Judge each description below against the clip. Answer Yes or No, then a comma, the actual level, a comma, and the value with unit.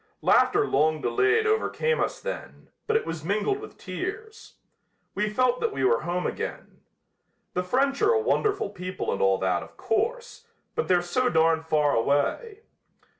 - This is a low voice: No, high, 240 Hz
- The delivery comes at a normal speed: Yes, average, 165 wpm